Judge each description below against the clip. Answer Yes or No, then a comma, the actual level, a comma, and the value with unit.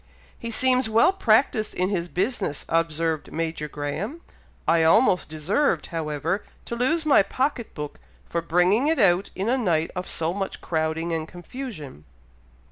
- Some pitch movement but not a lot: No, wide, 6.4 semitones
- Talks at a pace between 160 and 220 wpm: No, average, 150 wpm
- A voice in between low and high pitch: Yes, medium, 180 Hz